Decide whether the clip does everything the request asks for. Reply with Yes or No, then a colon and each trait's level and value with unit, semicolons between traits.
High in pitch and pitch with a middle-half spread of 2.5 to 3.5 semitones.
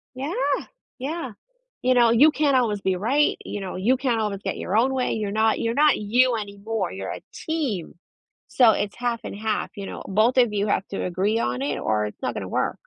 No: high, 220 Hz; average, 4.2 semitones